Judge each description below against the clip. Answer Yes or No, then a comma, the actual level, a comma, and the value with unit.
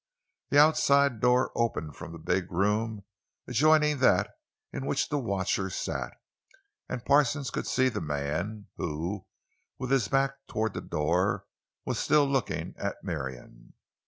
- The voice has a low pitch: Yes, low, 110 Hz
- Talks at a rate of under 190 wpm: Yes, average, 140 wpm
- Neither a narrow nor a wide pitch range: No, wide, 8.0 semitones